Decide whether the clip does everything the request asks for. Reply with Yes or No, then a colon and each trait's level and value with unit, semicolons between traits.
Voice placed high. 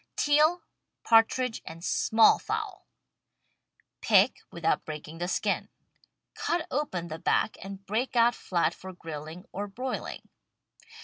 Yes: high, 205 Hz